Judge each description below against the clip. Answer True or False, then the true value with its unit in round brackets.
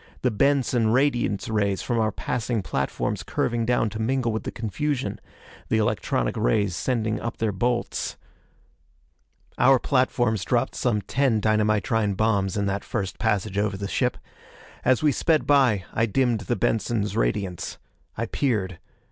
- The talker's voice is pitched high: False (110 Hz)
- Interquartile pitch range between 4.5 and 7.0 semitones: False (3.4 semitones)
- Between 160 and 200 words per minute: False (150 wpm)